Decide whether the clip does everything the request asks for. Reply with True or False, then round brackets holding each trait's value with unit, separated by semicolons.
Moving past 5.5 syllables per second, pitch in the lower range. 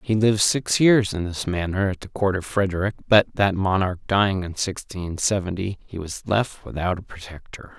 False (5.1 syllables/s; 95 Hz)